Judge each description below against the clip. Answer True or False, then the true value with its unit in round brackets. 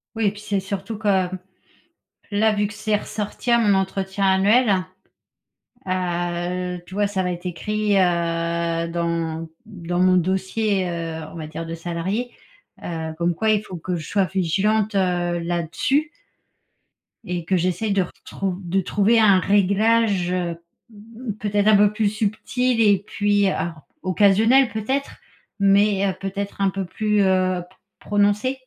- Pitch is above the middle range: True (195 Hz)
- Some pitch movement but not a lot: True (3.0 semitones)